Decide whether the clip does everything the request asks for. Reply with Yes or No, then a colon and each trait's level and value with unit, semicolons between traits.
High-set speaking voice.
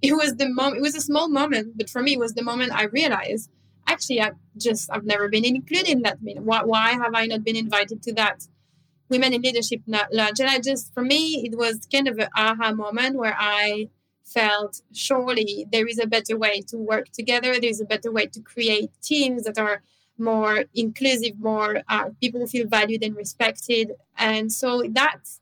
Yes: high, 225 Hz